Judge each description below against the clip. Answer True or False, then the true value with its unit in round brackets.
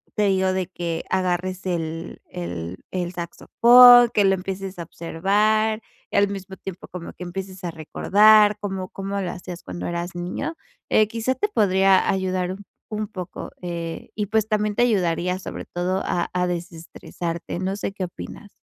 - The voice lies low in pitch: False (185 Hz)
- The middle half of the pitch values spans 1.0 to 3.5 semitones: True (2.8 semitones)